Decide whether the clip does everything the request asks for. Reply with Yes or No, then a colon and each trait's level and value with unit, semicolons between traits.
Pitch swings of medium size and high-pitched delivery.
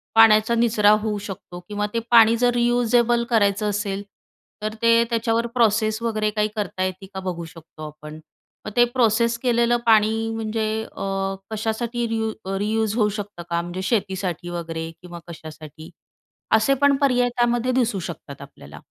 Yes: average, 3.8 semitones; high, 215 Hz